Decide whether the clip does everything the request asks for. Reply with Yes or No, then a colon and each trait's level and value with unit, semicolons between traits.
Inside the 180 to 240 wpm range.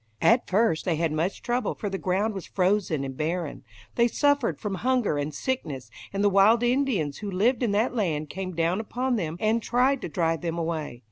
Yes: fast, 205 wpm